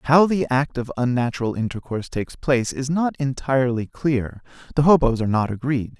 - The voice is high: No, low, 130 Hz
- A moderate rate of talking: Yes, average, 170 wpm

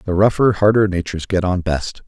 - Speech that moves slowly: No, average, 200 wpm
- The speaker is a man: Yes, male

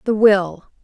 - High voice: Yes, high, 205 Hz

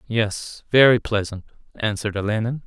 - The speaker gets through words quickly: No, slow, 115 wpm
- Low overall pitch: Yes, low, 110 Hz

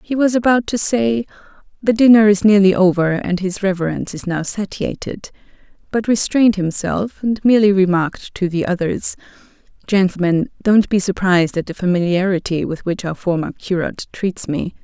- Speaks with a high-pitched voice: Yes, high, 195 Hz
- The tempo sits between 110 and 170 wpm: Yes, average, 160 wpm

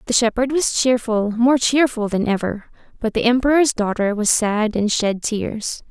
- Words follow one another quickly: No, average, 175 wpm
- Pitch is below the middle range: No, high, 230 Hz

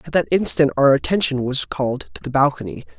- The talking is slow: No, average, 200 wpm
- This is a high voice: No, medium, 140 Hz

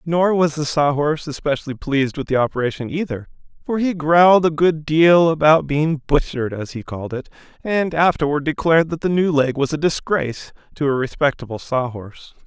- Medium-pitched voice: Yes, medium, 150 Hz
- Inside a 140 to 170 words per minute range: No, average, 190 wpm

